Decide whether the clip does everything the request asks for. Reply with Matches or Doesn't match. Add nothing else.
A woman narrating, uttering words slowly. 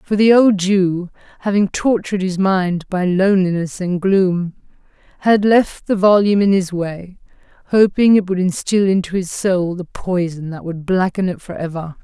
Doesn't match